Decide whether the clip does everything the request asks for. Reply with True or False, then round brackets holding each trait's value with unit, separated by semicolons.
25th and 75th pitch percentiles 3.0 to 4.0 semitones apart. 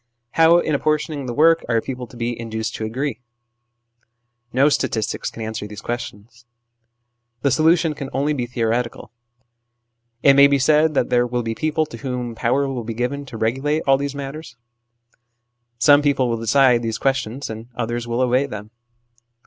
True (3.4 semitones)